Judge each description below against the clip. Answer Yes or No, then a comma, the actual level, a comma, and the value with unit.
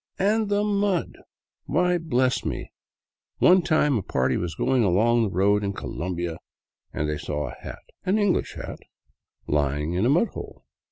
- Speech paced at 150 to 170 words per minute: Yes, average, 165 wpm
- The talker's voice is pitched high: No, low, 120 Hz